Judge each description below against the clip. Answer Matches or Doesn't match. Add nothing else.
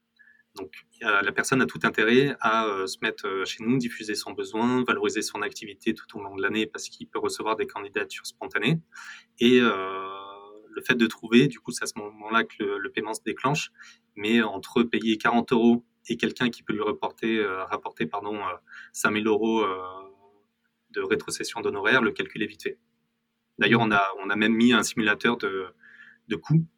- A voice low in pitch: Matches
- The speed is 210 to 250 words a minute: Doesn't match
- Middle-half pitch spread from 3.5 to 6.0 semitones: Doesn't match